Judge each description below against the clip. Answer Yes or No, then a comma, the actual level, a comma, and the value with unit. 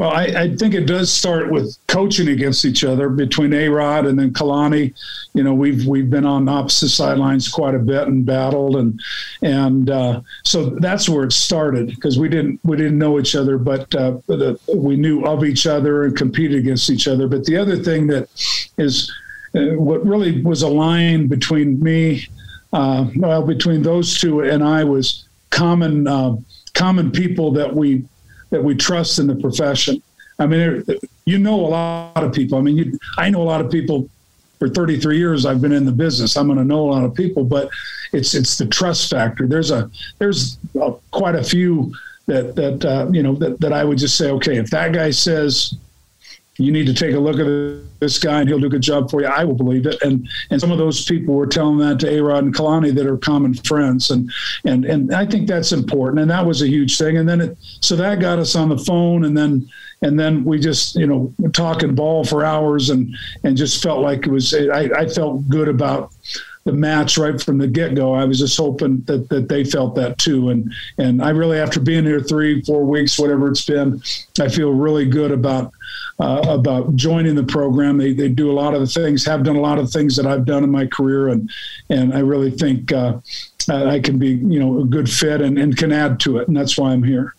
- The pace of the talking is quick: Yes, fast, 225 wpm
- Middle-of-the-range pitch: Yes, medium, 145 Hz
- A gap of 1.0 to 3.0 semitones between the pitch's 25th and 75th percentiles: Yes, narrow, 2.6 semitones